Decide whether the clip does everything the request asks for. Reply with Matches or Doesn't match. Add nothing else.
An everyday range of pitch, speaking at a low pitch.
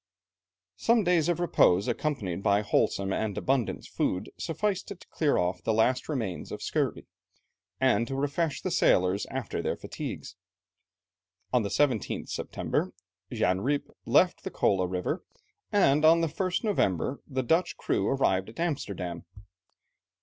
Doesn't match